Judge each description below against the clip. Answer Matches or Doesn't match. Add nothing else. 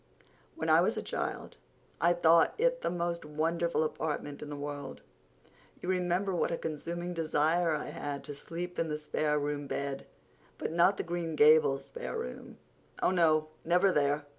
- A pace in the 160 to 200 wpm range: Matches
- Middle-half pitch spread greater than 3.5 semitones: Doesn't match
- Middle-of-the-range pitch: Matches